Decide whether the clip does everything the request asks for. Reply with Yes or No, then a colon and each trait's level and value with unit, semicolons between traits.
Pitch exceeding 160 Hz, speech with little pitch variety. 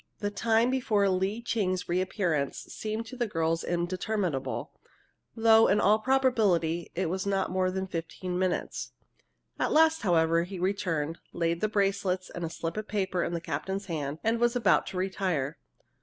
No: high, 190 Hz; average, 3.9 semitones